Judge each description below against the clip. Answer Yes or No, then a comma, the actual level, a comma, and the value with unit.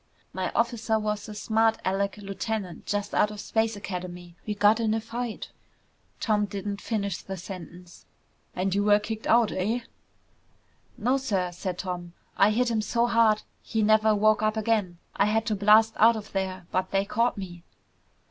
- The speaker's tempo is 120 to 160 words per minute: No, average, 175 wpm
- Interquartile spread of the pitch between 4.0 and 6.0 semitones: No, narrow, 2.5 semitones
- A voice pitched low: No, high, 210 Hz